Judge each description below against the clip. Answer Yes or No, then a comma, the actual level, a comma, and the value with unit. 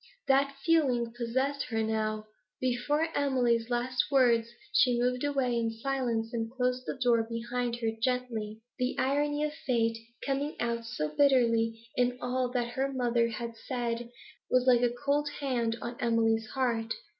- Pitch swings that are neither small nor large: No, narrow, 2.3 semitones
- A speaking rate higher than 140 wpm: Yes, average, 155 wpm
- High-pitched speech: Yes, high, 245 Hz